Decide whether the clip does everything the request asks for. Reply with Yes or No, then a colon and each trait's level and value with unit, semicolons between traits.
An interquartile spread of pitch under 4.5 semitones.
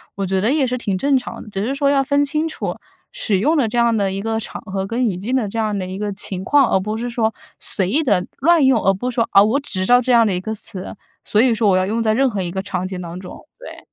No: average, 4.8 semitones